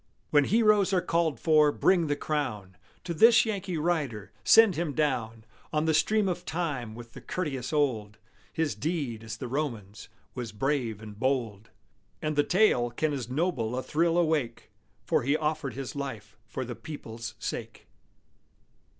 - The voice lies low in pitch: No, medium, 145 Hz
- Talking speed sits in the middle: Yes, average, 160 wpm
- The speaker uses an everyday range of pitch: No, wide, 6.0 semitones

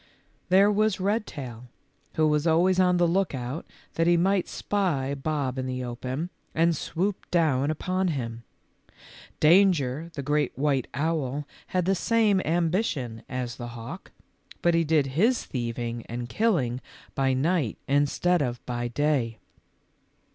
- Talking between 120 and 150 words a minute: Yes, average, 140 wpm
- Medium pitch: Yes, medium, 150 Hz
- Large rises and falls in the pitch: Yes, wide, 5.8 semitones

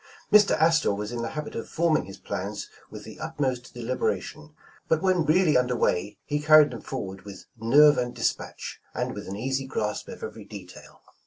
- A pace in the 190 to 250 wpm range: Yes, average, 195 wpm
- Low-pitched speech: Yes, low, 130 Hz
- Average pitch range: No, wide, 6.0 semitones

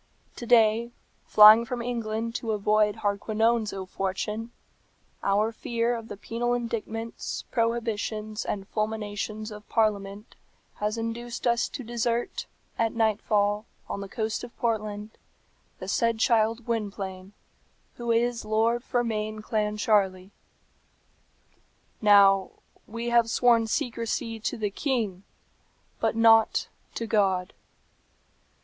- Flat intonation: Yes, narrow, 1.8 semitones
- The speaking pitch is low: No, high, 220 Hz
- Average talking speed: No, slow, 115 wpm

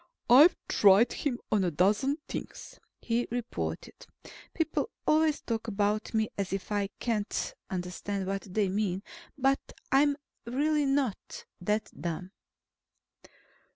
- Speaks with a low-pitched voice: No, high, 215 Hz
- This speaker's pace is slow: Yes, slow, 120 wpm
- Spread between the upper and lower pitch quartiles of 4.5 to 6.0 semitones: Yes, wide, 5.6 semitones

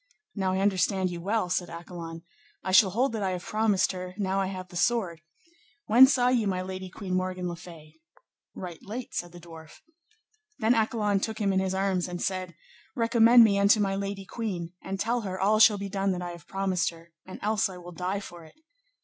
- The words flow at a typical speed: No, fast, 215 wpm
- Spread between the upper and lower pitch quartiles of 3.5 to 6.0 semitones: No, average, 2.8 semitones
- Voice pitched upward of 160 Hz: Yes, high, 190 Hz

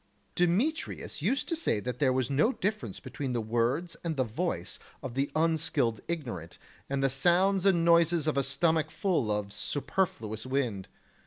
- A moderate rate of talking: Yes, average, 165 wpm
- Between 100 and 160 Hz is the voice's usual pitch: Yes, medium, 140 Hz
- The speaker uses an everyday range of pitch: No, wide, 6.1 semitones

